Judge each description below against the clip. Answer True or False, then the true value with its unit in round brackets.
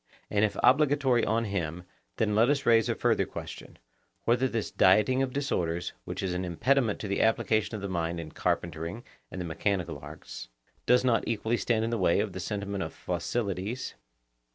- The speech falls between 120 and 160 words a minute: False (185 wpm)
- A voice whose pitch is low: True (105 Hz)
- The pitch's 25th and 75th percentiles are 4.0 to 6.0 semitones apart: True (4.8 semitones)